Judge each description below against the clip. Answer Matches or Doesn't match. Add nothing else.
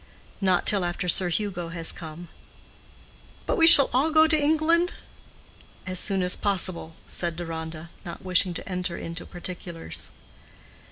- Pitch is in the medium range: Matches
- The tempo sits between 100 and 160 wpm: Matches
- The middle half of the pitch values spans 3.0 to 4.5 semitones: Matches